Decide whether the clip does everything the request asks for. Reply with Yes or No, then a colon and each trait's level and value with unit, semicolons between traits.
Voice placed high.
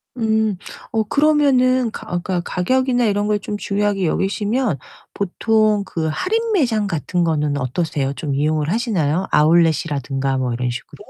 Yes: high, 195 Hz